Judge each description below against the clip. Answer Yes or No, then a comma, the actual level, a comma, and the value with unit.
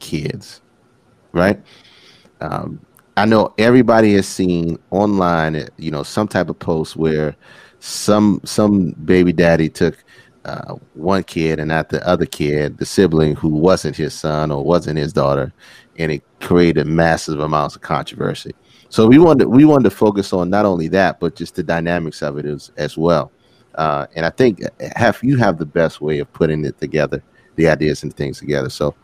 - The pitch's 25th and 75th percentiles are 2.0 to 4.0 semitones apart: Yes, average, 3.5 semitones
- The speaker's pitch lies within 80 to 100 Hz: Yes, very low, 85 Hz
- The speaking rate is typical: Yes, average, 180 wpm